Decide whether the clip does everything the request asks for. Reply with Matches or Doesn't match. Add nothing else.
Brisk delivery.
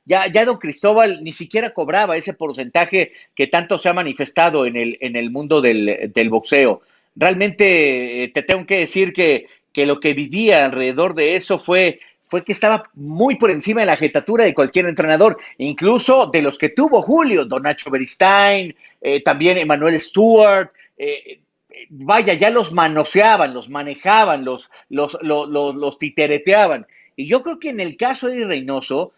Doesn't match